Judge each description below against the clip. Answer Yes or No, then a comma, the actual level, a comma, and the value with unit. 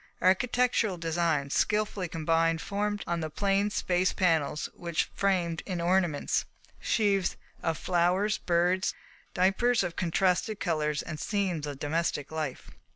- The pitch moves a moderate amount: Yes, average, 3.3 semitones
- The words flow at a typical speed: No, slow, 125 wpm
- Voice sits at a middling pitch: Yes, medium, 175 Hz